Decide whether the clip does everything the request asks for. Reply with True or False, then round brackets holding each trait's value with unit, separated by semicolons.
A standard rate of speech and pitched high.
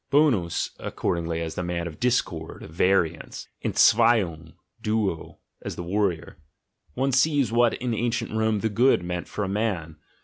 False (150 wpm; 100 Hz)